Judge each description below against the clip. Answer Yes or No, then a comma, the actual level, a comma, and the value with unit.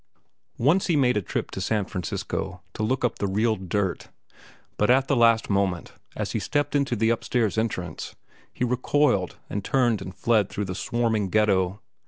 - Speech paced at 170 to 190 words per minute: Yes, average, 180 wpm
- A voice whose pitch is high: No, low, 110 Hz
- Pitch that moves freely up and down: No, average, 4.1 semitones